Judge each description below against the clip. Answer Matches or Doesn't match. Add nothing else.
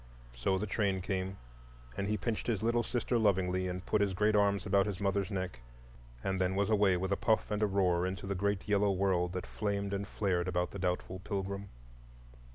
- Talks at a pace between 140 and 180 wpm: Doesn't match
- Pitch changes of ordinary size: Doesn't match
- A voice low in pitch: Matches